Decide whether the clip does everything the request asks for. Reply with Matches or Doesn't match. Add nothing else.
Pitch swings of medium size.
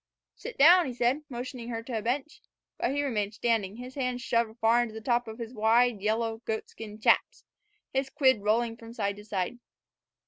Doesn't match